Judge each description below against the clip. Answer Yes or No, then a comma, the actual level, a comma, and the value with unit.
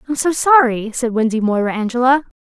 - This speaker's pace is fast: No, average, 175 wpm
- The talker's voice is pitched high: Yes, high, 245 Hz